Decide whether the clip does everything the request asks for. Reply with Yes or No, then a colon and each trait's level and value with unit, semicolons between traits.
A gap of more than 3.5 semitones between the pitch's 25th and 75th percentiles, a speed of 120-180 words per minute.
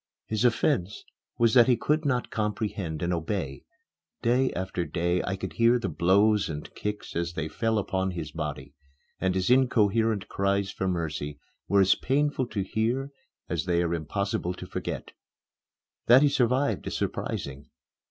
Yes: average, 5.3 semitones; average, 160 wpm